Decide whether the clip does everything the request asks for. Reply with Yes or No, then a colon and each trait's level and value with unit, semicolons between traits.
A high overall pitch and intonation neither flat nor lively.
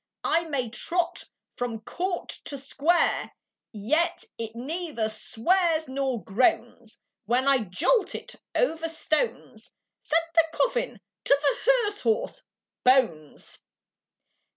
No: very high, 285 Hz; wide, 6.5 semitones